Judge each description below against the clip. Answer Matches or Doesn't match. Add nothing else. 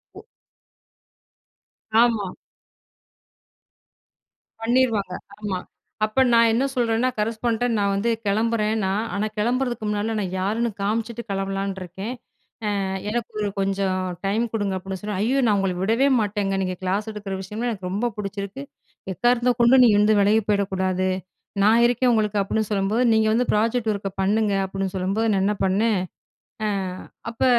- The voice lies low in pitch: Doesn't match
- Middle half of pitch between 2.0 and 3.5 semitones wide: Matches